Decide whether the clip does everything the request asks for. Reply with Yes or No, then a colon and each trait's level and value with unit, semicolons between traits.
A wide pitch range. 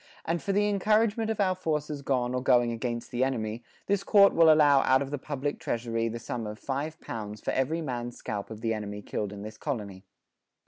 Yes: wide, 5.9 semitones